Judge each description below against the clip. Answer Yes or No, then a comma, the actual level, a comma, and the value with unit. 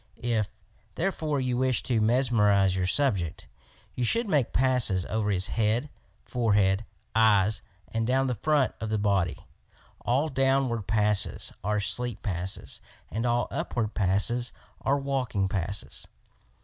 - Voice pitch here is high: No, low, 115 Hz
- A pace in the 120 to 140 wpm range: Yes, slow, 135 wpm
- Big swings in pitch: No, average, 4.1 semitones